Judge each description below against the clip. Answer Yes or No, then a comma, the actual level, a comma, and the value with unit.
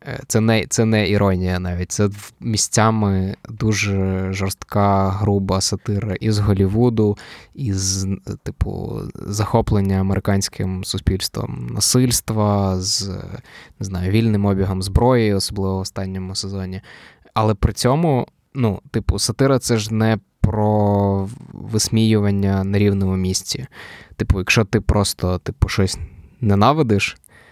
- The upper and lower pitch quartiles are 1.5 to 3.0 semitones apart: Yes, narrow, 2.5 semitones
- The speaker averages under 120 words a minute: Yes, average, 110 wpm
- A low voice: Yes, low, 100 Hz